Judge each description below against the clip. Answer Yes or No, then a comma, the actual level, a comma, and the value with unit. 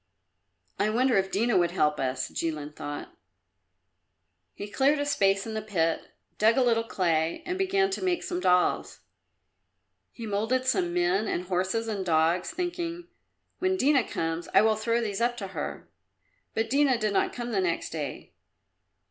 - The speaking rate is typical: Yes, average, 165 wpm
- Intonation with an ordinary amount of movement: No, wide, 6.5 semitones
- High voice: Yes, high, 215 Hz